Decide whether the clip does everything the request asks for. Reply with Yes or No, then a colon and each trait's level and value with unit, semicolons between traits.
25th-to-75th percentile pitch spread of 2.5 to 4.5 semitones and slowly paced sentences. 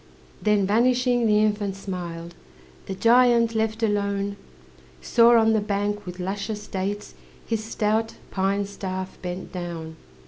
Yes: average, 2.8 semitones; slow, 130 wpm